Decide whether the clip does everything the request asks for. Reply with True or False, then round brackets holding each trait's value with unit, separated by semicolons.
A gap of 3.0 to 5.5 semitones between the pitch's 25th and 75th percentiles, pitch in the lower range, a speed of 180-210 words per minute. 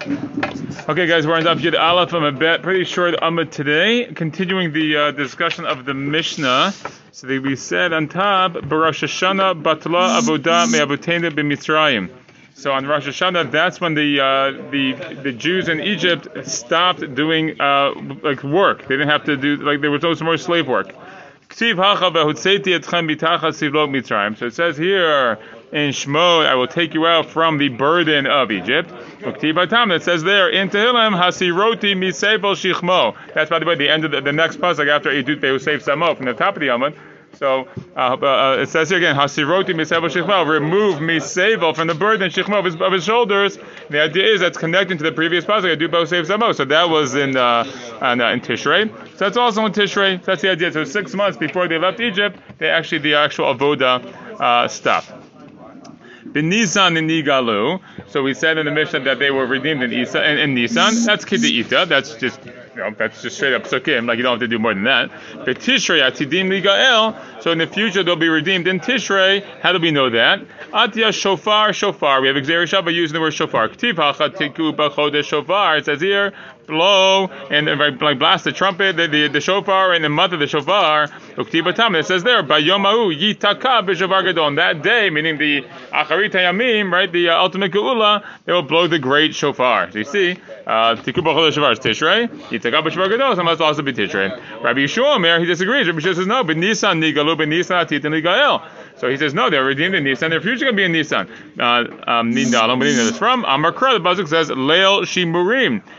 False (4.3 semitones; 165 Hz; 190 wpm)